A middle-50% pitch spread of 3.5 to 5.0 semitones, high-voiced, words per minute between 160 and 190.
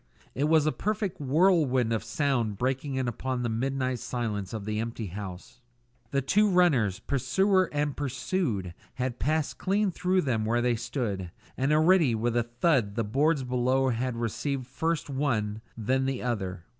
No: average, 4.5 semitones; low, 130 Hz; average, 165 wpm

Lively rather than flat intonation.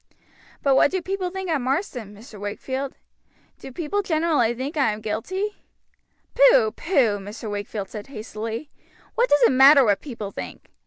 Yes: wide, 7.8 semitones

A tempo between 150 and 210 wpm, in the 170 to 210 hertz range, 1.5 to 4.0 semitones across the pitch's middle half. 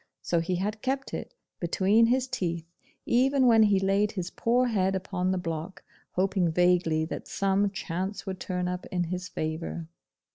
Yes: average, 170 wpm; medium, 185 Hz; average, 2.9 semitones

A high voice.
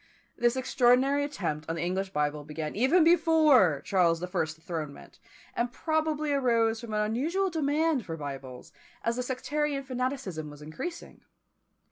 Yes: high, 235 Hz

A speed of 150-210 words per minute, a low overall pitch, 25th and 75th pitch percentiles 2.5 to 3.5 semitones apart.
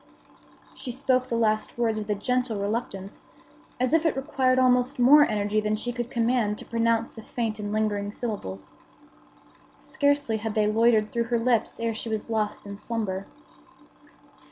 No: average, 165 wpm; high, 230 Hz; average, 2.8 semitones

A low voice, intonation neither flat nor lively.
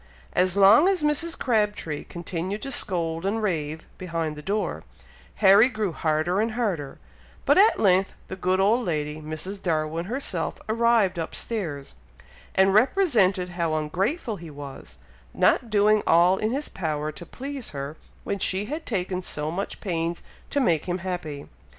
No: medium, 185 Hz; average, 4.9 semitones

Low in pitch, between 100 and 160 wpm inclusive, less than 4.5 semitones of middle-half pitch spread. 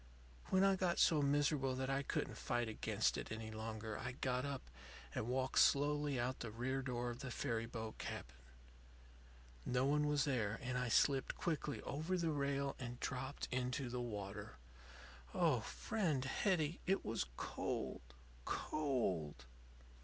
Yes: low, 130 Hz; average, 155 wpm; average, 3.6 semitones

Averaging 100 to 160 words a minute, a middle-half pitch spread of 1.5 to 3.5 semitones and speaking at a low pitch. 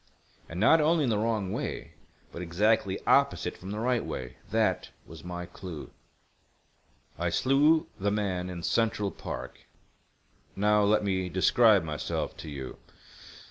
No: average, 140 wpm; average, 4.1 semitones; low, 100 Hz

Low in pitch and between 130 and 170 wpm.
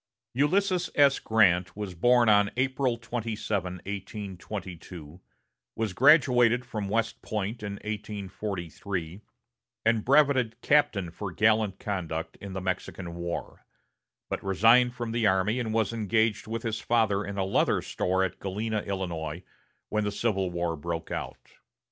Yes: low, 105 Hz; slow, 135 wpm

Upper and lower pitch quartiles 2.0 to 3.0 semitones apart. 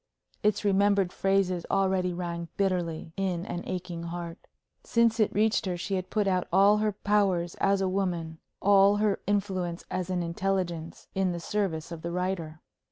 Yes: narrow, 2.4 semitones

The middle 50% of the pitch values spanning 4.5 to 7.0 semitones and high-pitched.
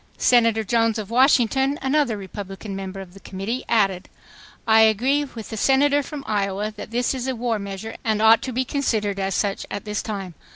No: average, 4.1 semitones; high, 220 Hz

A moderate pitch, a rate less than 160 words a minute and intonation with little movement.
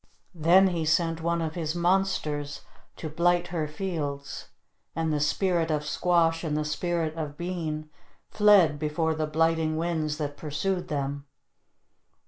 Yes: medium, 160 Hz; average, 140 wpm; narrow, 2.3 semitones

